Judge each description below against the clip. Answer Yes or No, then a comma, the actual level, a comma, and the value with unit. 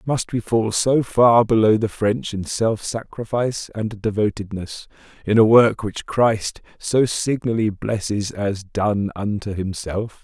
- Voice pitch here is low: Yes, low, 110 Hz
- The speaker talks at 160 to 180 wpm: No, average, 145 wpm